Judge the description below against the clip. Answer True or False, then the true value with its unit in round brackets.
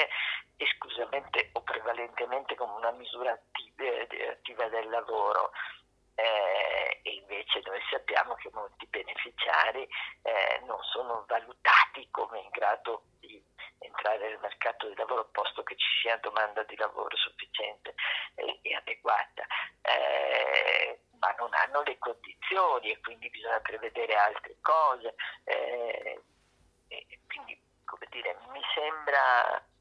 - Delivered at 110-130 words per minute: True (120 wpm)